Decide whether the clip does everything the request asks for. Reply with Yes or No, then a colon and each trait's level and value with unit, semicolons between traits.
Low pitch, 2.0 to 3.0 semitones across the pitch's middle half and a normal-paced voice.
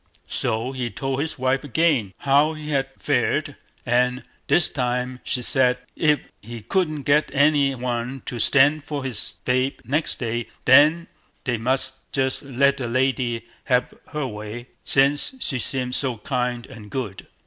Yes: low, 130 Hz; average, 2.7 semitones; average, 150 wpm